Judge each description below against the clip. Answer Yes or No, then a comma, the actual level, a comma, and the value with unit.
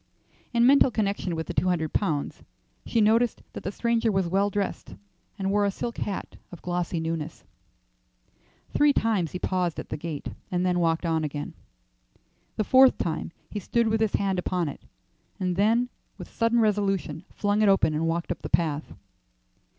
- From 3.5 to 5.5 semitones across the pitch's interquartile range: Yes, average, 4.5 semitones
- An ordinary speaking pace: Yes, average, 180 wpm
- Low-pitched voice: No, high, 190 Hz